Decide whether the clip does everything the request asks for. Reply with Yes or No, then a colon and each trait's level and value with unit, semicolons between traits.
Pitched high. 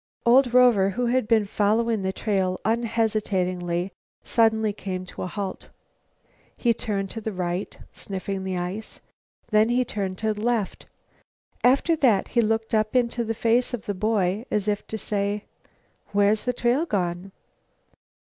Yes: high, 215 Hz